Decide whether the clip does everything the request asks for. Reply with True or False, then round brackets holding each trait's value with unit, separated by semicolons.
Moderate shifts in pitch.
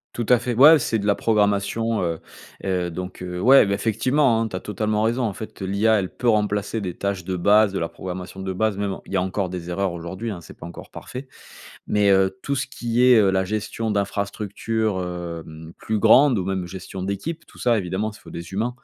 True (3.2 semitones)